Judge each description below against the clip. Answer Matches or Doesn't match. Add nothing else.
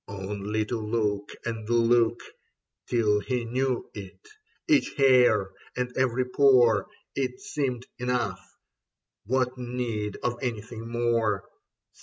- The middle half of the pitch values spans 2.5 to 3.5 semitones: Matches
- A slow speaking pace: Matches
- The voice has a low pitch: Matches